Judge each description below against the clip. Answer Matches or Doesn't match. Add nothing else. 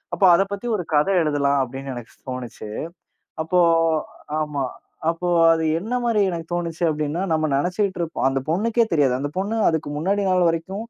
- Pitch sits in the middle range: Matches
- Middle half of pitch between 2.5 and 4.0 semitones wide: Doesn't match